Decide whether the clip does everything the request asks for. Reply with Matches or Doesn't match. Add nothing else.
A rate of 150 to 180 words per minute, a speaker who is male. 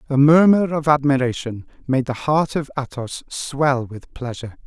Matches